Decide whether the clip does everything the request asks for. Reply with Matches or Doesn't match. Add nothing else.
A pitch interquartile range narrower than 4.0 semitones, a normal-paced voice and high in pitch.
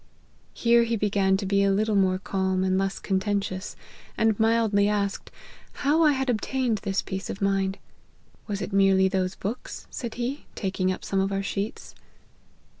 Matches